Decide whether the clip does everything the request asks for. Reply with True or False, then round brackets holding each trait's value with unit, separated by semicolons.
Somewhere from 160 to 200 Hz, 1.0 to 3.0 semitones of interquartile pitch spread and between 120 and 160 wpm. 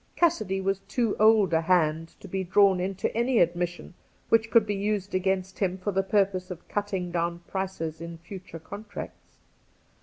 False (190 Hz; 2.6 semitones; 170 wpm)